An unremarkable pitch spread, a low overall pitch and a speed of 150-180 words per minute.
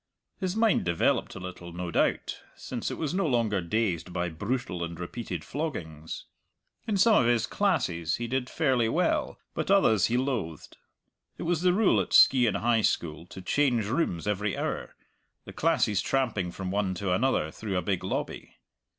No: wide, 6.9 semitones; low, 110 Hz; average, 175 wpm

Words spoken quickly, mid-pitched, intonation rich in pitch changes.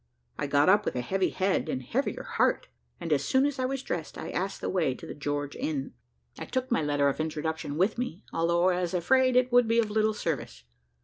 Yes: fast, 235 wpm; medium, 180 Hz; wide, 7.9 semitones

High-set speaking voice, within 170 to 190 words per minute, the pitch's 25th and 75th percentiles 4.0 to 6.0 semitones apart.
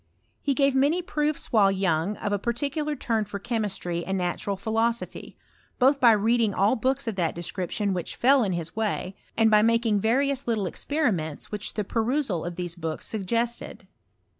Yes: high, 220 Hz; average, 180 wpm; average, 4.7 semitones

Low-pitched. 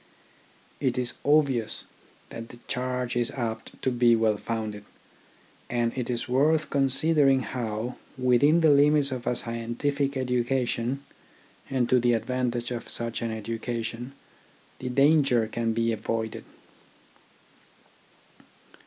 Yes: low, 125 Hz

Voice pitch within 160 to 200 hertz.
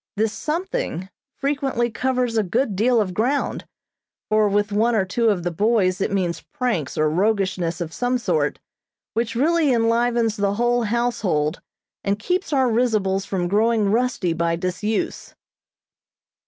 No: high, 220 Hz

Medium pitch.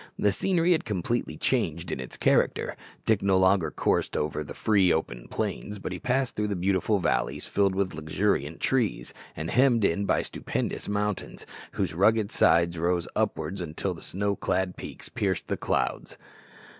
No: very low, 95 Hz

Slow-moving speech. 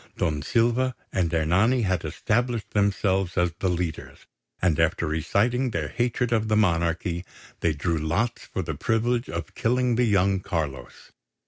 No: average, 150 wpm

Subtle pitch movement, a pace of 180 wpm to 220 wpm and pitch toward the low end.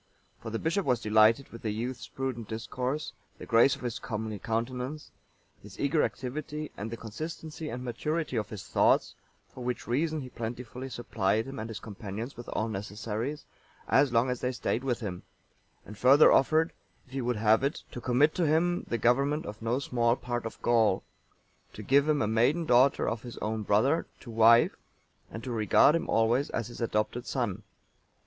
No: average, 3.4 semitones; average, 185 wpm; low, 120 Hz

